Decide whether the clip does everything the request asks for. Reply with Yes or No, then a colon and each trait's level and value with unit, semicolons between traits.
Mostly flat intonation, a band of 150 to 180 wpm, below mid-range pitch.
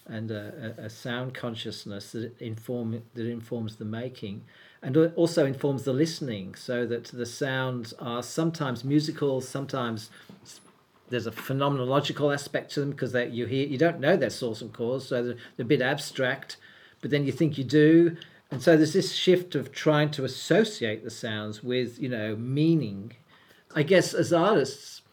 No: average, 4.3 semitones; average, 170 wpm; low, 130 Hz